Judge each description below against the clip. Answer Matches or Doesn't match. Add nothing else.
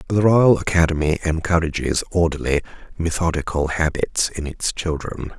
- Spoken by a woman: Doesn't match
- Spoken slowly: Matches